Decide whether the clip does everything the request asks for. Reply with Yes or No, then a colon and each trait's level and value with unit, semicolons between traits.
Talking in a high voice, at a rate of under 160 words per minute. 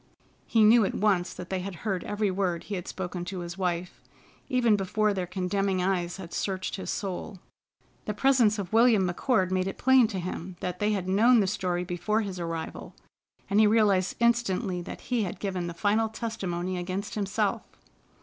No: high, 195 Hz; average, 190 wpm